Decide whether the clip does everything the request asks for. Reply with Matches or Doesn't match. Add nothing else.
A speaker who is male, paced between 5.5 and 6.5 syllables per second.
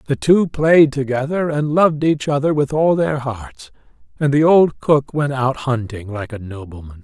Doesn't match